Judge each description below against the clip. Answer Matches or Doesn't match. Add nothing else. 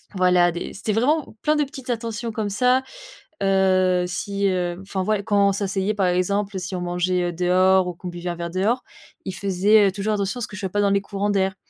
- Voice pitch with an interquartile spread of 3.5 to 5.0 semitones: Doesn't match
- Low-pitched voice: Doesn't match